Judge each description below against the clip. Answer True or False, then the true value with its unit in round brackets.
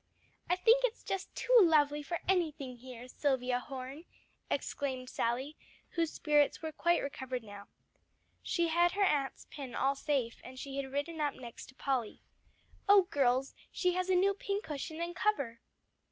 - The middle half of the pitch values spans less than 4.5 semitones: False (5.0 semitones)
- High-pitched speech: True (290 Hz)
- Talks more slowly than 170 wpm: True (160 wpm)